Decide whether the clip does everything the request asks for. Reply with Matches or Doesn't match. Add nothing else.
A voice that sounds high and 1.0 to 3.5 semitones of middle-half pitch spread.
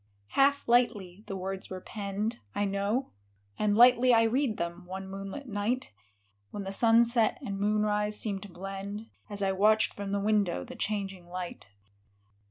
Matches